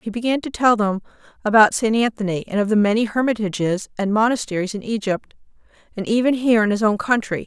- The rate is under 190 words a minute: No, average, 195 wpm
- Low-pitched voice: No, high, 215 Hz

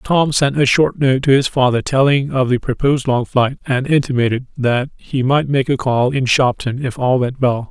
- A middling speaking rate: No, fast, 220 wpm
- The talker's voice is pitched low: Yes, low, 130 Hz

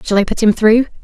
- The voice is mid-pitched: No, high, 220 Hz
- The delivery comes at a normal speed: No, fast, 290 wpm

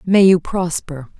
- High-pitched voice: No, medium, 175 Hz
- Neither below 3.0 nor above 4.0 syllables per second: Yes, 3.9 syllables/s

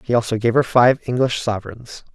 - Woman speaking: No, male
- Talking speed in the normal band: Yes, average, 195 wpm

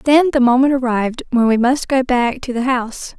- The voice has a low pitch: No, very high, 250 Hz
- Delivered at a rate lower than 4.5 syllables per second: No, 5.2 syllables/s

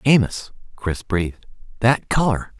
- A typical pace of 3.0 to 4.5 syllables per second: Yes, 4.2 syllables/s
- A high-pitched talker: No, low, 110 Hz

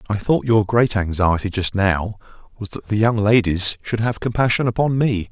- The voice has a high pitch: No, low, 105 Hz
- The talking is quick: No, average, 190 wpm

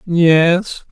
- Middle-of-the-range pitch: Yes, medium, 170 Hz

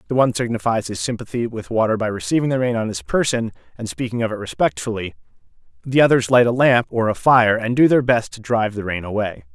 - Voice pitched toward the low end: Yes, low, 115 Hz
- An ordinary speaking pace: No, fast, 225 wpm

